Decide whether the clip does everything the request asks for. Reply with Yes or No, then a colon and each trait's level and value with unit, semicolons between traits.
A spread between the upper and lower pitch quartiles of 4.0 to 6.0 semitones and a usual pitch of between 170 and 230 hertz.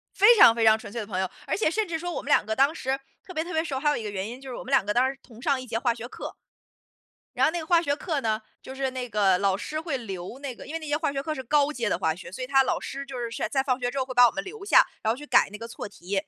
No: average, 4.9 semitones; very high, 260 Hz